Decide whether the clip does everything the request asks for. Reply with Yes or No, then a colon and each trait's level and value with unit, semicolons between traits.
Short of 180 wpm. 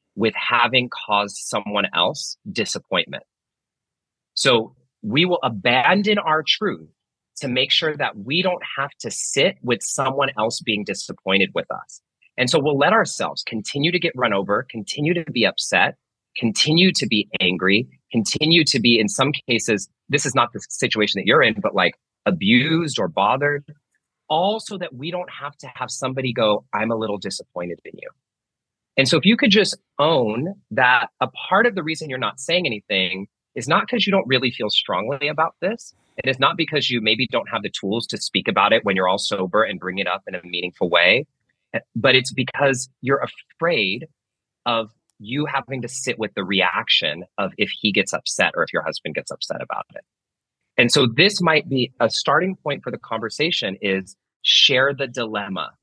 No: average, 190 wpm